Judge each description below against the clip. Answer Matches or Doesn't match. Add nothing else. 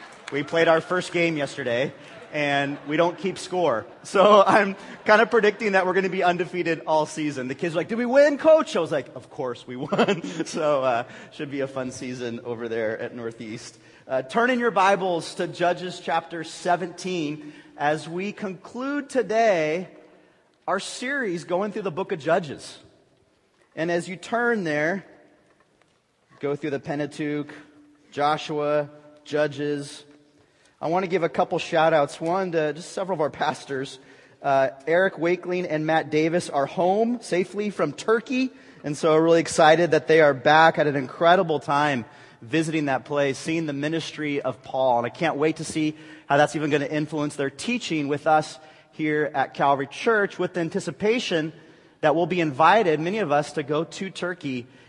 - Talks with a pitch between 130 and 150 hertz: Doesn't match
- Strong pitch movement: Doesn't match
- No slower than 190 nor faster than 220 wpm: Doesn't match